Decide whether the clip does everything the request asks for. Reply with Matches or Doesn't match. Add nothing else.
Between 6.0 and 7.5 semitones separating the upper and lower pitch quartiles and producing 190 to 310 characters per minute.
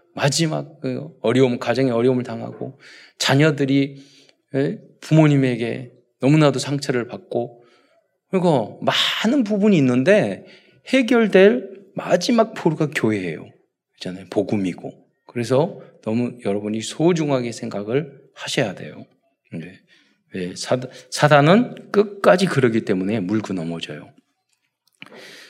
Matches